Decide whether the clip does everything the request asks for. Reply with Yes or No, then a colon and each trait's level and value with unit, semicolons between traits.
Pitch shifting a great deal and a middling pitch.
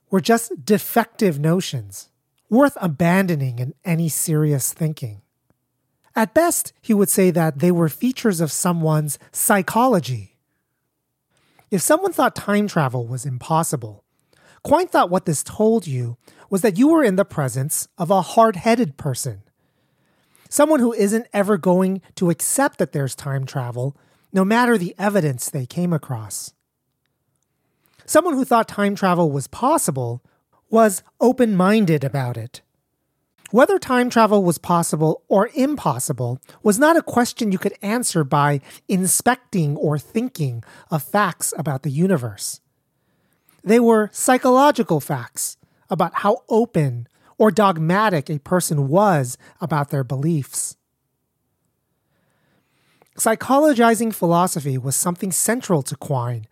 Yes: wide, 7.4 semitones; medium, 175 Hz